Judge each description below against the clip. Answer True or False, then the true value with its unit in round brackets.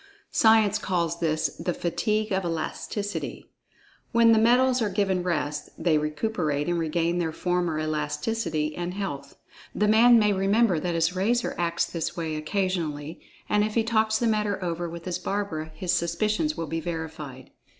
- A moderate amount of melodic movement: True (4.7 semitones)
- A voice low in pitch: False (175 Hz)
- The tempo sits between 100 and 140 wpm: False (160 wpm)